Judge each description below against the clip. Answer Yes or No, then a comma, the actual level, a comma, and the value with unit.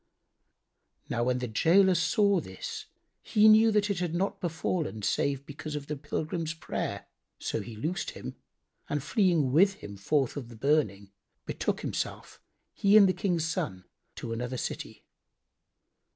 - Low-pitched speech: No, medium, 155 Hz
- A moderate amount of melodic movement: No, wide, 6.9 semitones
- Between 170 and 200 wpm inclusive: No, average, 150 wpm